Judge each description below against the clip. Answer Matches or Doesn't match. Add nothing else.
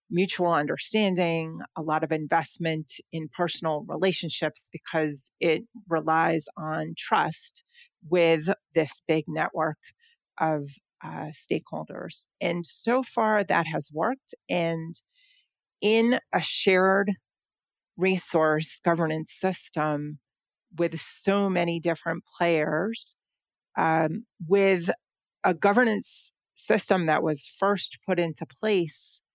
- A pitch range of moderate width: Matches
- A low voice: Doesn't match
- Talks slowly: Matches